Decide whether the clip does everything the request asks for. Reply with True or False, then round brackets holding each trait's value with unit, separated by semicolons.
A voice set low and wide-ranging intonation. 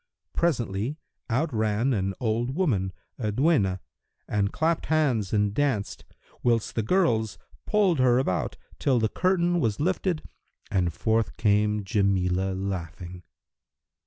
True (110 Hz; 6.6 semitones)